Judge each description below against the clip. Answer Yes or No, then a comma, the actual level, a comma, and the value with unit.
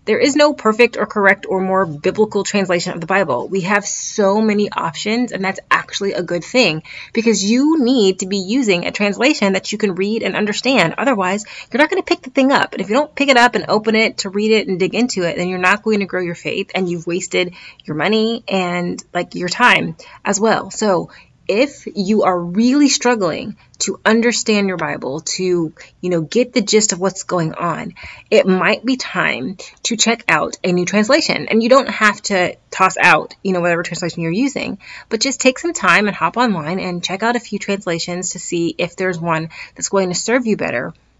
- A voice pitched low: No, high, 200 Hz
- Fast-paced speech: Yes, fast, 220 wpm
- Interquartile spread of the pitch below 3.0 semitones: No, average, 4.1 semitones